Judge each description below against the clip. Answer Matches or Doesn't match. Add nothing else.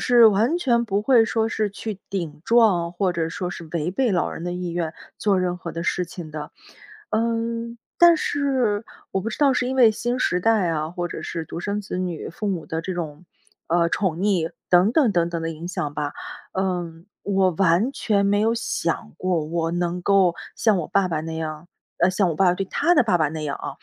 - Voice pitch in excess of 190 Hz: Doesn't match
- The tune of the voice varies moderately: Matches